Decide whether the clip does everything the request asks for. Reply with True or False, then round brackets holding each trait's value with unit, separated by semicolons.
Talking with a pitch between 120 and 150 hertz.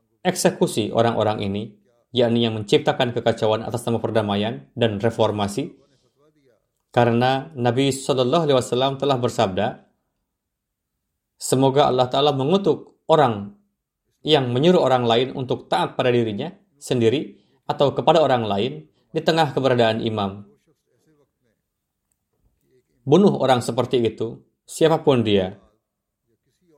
True (125 Hz)